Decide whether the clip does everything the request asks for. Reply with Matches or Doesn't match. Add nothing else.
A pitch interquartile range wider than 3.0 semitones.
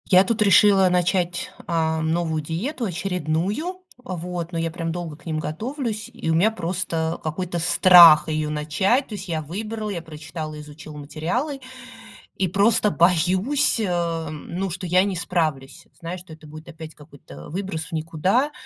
Matches